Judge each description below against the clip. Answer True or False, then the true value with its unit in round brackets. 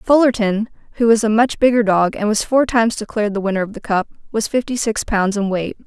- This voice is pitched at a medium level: False (220 Hz)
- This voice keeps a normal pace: False (235 wpm)